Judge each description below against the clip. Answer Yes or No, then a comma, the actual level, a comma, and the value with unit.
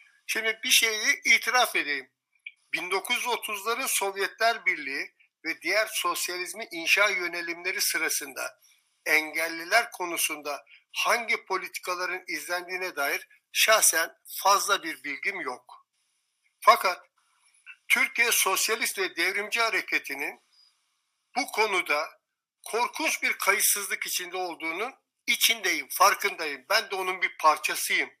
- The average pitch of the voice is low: No, high, 205 Hz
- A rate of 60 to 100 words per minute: Yes, slow, 95 wpm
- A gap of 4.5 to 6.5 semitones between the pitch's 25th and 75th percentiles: Yes, average, 5.2 semitones